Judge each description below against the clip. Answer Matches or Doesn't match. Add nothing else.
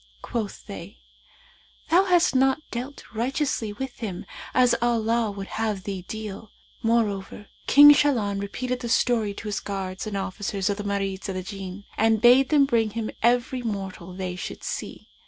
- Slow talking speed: Doesn't match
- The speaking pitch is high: Matches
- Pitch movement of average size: Matches